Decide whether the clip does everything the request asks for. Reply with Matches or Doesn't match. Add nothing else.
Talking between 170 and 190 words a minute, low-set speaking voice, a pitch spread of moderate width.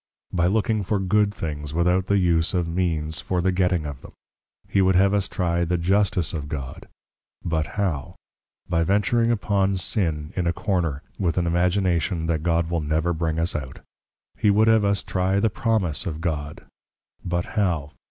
Matches